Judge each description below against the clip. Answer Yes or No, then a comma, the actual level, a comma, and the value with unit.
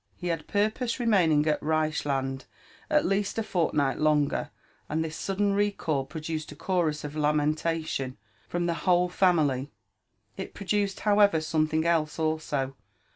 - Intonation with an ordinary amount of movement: Yes, average, 3.9 semitones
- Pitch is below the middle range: No, medium, 160 Hz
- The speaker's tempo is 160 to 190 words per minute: No, slow, 135 wpm